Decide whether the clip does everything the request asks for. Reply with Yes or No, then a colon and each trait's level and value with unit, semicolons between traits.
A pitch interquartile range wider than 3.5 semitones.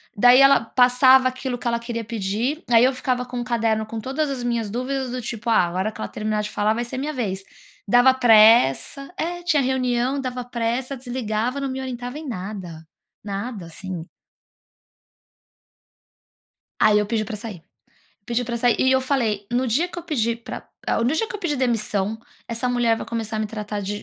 No: average, 3.2 semitones